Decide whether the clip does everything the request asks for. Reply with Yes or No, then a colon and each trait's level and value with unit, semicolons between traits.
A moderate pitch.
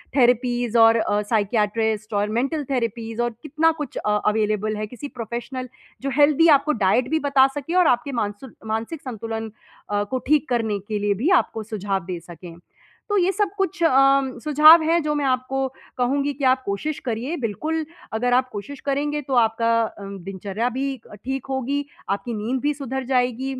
No: high, 245 Hz